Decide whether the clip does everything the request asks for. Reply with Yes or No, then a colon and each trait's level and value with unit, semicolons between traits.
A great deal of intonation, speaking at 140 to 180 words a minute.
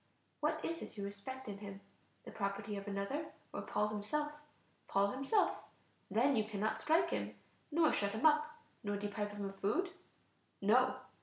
Yes: wide, 6.7 semitones; average, 165 wpm